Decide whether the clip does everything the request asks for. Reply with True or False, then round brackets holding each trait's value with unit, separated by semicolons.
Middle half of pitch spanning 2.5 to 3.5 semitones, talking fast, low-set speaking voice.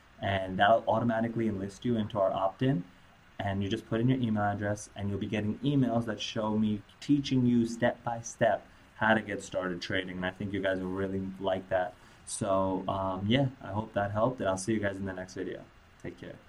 True (3.0 semitones; 230 wpm; 100 Hz)